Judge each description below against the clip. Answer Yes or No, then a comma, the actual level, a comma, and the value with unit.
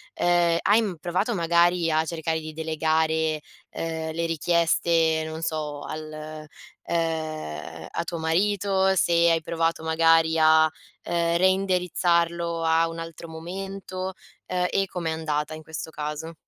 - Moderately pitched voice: Yes, medium, 165 Hz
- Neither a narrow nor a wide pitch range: No, narrow, 1.5 semitones